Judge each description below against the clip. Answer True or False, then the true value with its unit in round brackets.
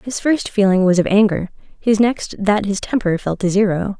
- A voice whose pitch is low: False (205 Hz)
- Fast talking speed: True (210 wpm)